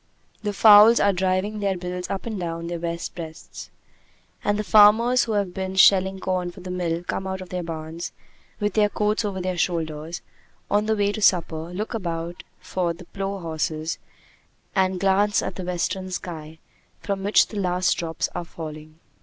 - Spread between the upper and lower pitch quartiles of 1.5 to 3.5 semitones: Yes, average, 3.0 semitones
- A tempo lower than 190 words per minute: Yes, average, 180 wpm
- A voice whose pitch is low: No, medium, 185 Hz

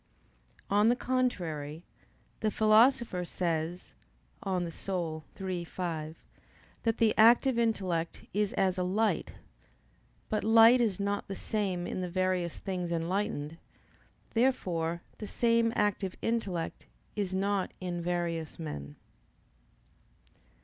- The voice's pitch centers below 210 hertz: Yes, medium, 185 Hz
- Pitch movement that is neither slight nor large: Yes, average, 4.1 semitones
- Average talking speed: No, slow, 115 wpm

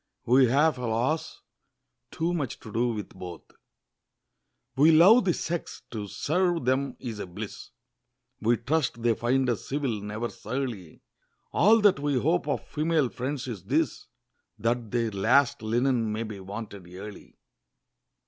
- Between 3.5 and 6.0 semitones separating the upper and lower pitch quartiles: Yes, average, 5.1 semitones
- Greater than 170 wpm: No, average, 145 wpm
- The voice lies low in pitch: Yes, low, 125 Hz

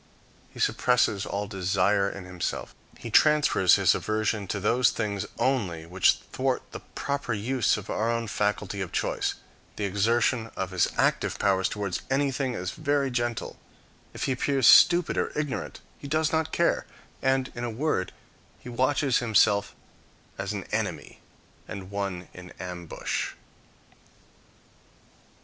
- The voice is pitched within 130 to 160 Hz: No, low, 110 Hz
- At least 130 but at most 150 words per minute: Yes, average, 140 wpm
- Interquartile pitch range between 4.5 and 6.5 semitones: Yes, average, 5.2 semitones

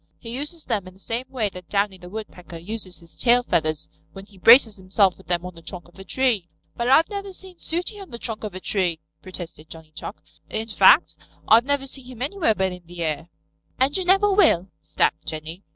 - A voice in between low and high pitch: No, high, 205 Hz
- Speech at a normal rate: No, fast, 220 wpm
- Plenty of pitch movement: Yes, wide, 6.5 semitones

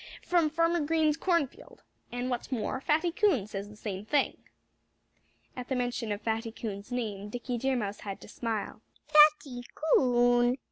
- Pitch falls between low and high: No, high, 245 Hz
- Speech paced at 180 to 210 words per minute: No, average, 155 wpm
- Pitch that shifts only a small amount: No, wide, 5.4 semitones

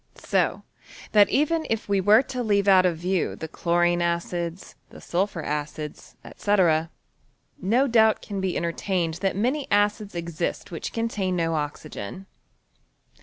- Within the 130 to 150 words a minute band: Yes, average, 145 wpm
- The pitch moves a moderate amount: Yes, average, 3.6 semitones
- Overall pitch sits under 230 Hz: Yes, high, 190 Hz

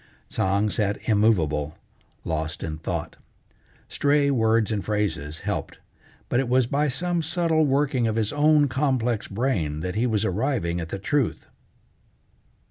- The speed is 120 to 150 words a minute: Yes, average, 140 wpm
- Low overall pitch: Yes, low, 110 Hz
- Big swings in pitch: Yes, wide, 6.5 semitones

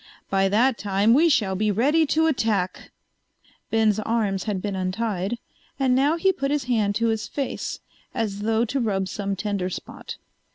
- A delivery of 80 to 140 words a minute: No, average, 170 wpm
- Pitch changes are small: No, average, 4.3 semitones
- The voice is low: No, high, 220 Hz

